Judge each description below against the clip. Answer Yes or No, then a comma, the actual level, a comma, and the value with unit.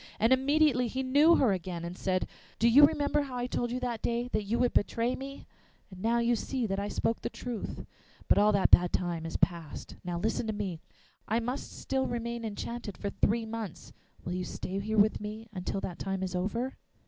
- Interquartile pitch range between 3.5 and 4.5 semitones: Yes, average, 4.2 semitones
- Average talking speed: No, fast, 210 wpm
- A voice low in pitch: No, high, 225 Hz